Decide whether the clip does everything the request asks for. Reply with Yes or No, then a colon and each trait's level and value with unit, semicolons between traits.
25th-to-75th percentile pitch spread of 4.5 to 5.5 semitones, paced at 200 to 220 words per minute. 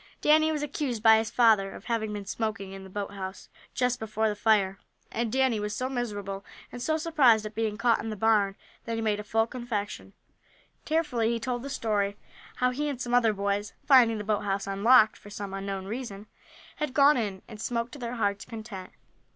No: average, 3.3 semitones; fast, 205 wpm